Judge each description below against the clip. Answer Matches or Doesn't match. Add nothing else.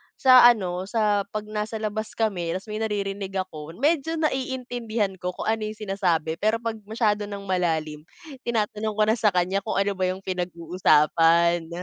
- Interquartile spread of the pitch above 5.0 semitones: Doesn't match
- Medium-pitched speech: Doesn't match